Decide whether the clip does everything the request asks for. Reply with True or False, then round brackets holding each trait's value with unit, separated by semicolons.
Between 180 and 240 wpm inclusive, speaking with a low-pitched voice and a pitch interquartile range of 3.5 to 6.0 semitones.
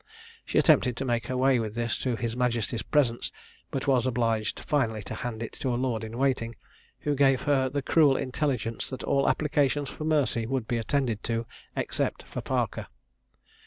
False (185 wpm; 125 Hz; 2.8 semitones)